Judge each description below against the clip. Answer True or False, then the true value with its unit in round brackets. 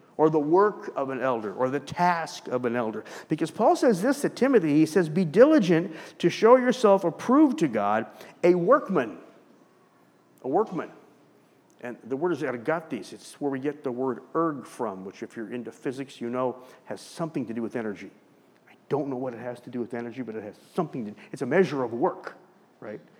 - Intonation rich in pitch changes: True (6.3 semitones)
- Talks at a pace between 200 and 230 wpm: True (205 wpm)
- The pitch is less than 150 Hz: True (140 Hz)